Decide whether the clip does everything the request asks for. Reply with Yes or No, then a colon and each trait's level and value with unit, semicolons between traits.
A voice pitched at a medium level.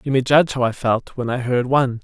No: low, 125 Hz